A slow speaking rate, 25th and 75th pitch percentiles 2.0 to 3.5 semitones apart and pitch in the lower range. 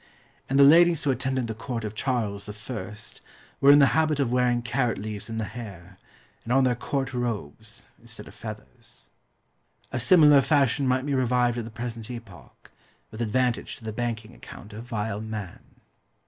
No: average, 175 wpm; average, 3.2 semitones; low, 120 Hz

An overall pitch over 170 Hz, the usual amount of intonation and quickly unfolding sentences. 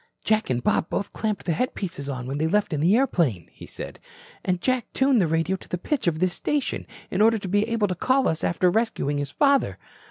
No: medium, 185 Hz; wide, 6.1 semitones; fast, 230 wpm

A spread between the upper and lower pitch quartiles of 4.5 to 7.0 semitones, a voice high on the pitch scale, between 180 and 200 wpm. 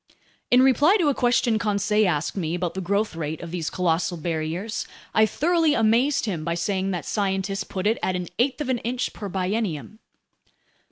Yes: average, 5.1 semitones; high, 200 Hz; average, 185 wpm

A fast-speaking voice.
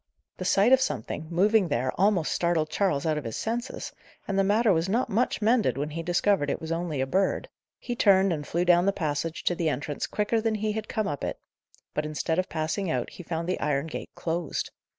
Yes: fast, 225 wpm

